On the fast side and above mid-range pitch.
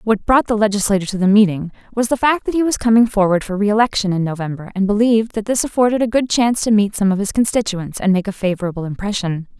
Yes: fast, 240 wpm; high, 210 Hz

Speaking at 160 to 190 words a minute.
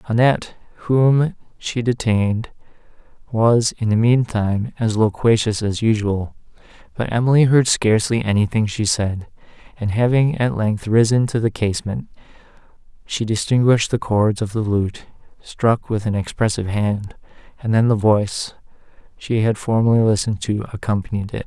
No: average, 145 wpm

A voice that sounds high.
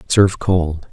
No: very low, 90 Hz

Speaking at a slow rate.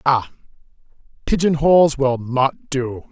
Yes: slow, 115 wpm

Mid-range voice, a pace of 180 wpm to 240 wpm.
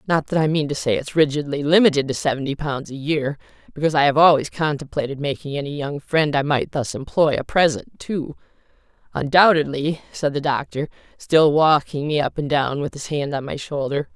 Yes: medium, 150 Hz; average, 195 wpm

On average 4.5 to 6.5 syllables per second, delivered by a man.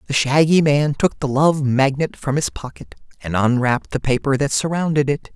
Yes: 5.1 syllables/s; male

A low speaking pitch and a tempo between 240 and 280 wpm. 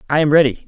No: medium, 145 Hz; fast, 265 wpm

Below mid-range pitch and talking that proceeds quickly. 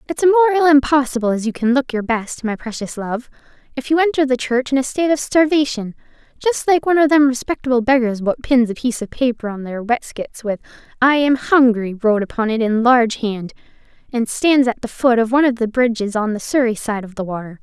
No: very high, 250 Hz; fast, 230 wpm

